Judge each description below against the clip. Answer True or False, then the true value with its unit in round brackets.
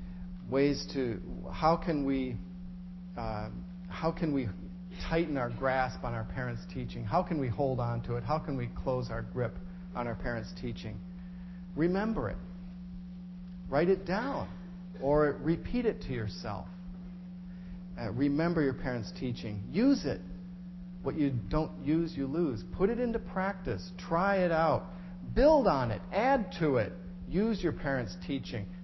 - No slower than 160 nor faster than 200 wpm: False (150 wpm)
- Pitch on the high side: False (165 Hz)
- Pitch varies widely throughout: True (5.9 semitones)